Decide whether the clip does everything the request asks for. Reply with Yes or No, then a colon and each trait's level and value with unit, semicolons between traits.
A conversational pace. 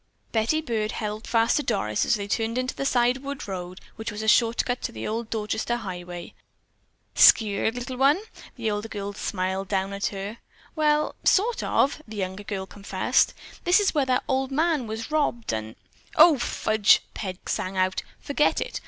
Yes: average, 180 wpm